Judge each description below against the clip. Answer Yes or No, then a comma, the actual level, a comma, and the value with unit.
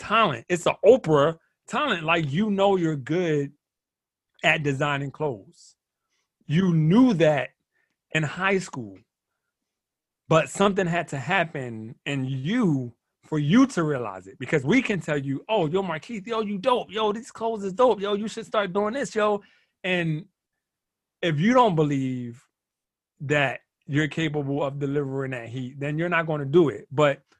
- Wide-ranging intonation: Yes, wide, 5.8 semitones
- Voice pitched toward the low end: No, medium, 160 Hz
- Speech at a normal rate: Yes, average, 165 wpm